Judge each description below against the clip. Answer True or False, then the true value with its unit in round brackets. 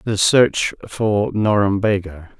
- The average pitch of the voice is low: True (105 Hz)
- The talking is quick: False (100 wpm)